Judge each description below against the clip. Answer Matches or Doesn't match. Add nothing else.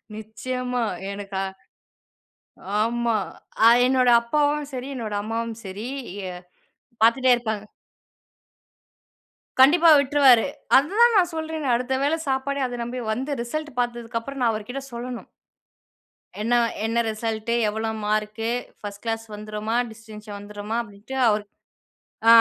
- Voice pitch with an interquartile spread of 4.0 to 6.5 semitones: Doesn't match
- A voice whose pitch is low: Doesn't match